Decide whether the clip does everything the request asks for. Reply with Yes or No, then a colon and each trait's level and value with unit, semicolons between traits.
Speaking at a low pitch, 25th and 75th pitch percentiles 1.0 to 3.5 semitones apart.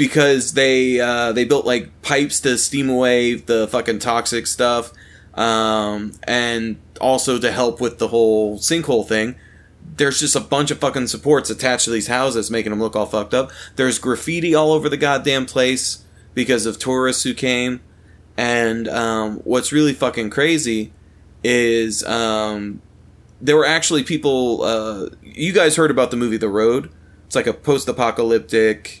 Yes: low, 120 Hz; average, 3.1 semitones